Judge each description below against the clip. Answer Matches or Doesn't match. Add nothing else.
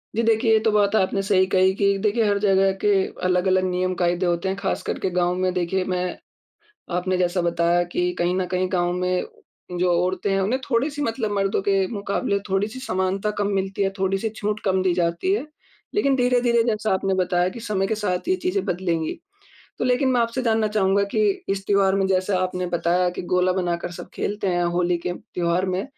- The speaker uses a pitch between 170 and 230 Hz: Matches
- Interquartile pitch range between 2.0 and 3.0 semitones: Matches